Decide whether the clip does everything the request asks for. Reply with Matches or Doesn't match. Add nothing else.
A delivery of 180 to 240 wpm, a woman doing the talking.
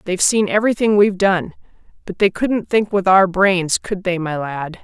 Matches